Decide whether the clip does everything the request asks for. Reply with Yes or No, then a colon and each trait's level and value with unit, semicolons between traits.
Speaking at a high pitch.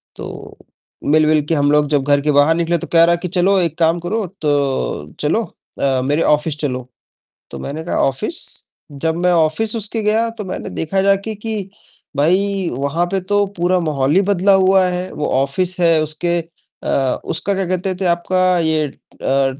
No: medium, 170 Hz